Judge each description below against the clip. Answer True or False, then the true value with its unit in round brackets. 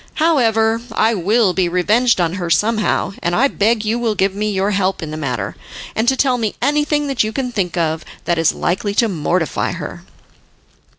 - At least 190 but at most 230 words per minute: True (195 wpm)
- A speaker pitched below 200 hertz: False (210 Hz)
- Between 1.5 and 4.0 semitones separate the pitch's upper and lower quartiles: False (4.8 semitones)